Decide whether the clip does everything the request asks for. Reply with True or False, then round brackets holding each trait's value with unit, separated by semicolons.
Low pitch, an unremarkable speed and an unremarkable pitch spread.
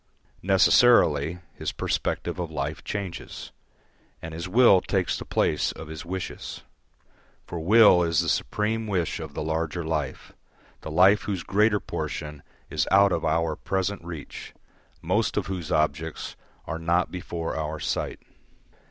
True (85 Hz; 145 wpm; 3.3 semitones)